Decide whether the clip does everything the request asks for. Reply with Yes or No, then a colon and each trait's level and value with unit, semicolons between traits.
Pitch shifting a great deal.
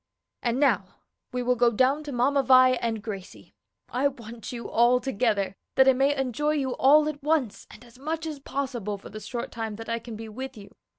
No: average, 3.2 semitones